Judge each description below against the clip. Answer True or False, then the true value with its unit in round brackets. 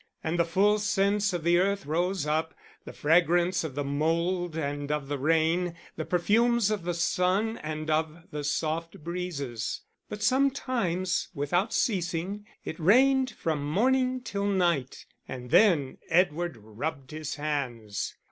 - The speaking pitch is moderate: True (170 Hz)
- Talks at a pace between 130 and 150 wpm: True (145 wpm)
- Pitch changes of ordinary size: True (4.5 semitones)